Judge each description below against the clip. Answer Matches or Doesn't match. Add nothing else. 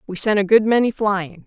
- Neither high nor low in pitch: Doesn't match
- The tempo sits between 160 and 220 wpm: Doesn't match